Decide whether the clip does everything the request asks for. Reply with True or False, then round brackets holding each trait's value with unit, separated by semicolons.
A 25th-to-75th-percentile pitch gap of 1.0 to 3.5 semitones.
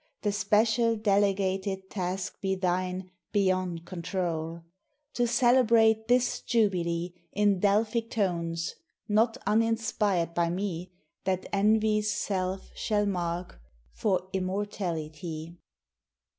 True (3.2 semitones)